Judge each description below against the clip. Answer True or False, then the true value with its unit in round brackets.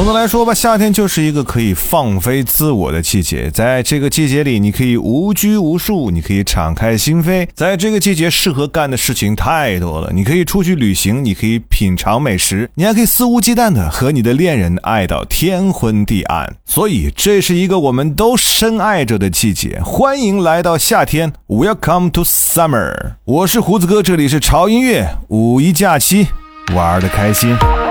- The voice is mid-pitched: True (145 Hz)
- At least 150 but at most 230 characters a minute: False (310 characters per minute)